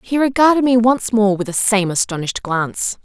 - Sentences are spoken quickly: No, average, 195 wpm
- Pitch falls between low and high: No, high, 220 Hz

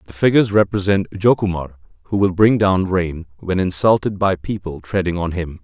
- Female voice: No, male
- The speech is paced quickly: No, average, 170 wpm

